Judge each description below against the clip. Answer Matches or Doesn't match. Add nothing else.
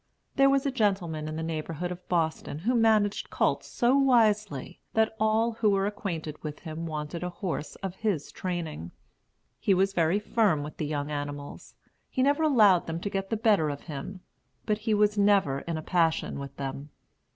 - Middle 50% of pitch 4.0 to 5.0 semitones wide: Doesn't match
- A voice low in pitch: Doesn't match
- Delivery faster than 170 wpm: Matches